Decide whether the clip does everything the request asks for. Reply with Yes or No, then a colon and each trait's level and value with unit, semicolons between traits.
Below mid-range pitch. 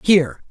No: medium, 180 Hz